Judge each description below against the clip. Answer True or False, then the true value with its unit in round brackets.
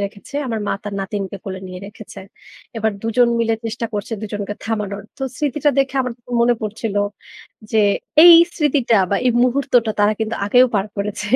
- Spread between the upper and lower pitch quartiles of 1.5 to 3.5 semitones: True (3.1 semitones)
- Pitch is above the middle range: True (220 Hz)